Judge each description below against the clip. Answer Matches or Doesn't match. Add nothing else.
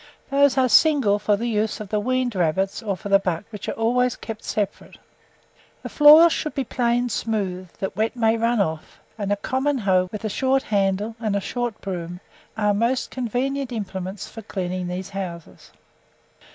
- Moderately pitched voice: Doesn't match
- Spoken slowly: Doesn't match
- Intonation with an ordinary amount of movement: Matches